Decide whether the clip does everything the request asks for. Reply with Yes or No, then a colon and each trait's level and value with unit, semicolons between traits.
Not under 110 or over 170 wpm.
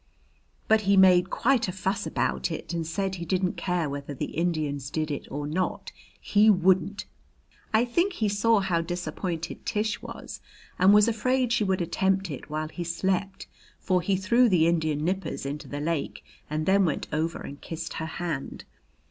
No: average, 180 wpm